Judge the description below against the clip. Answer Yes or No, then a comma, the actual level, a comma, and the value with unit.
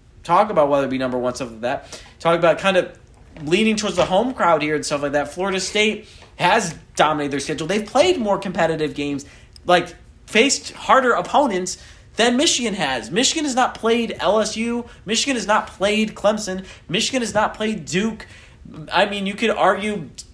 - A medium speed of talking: Yes, average, 185 wpm